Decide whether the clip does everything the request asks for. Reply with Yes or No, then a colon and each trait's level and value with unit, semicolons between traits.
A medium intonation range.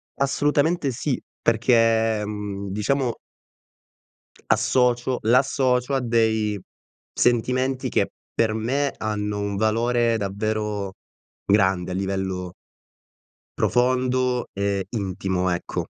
Yes: average, 3.8 semitones